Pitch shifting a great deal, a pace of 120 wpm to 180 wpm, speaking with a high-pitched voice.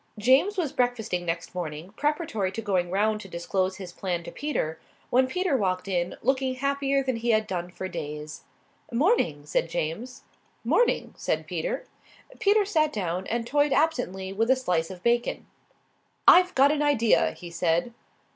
Yes: wide, 7.6 semitones; average, 165 wpm; high, 220 Hz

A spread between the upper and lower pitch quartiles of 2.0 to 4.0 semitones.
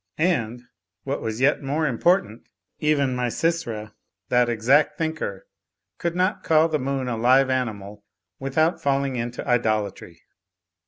No: average, 5.1 semitones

